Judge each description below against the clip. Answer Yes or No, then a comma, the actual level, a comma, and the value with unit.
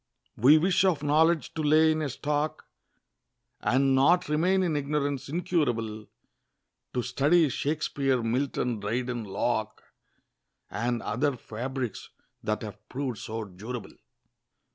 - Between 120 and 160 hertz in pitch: Yes, low, 135 Hz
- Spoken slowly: Yes, slow, 120 wpm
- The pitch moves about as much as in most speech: Yes, average, 4.7 semitones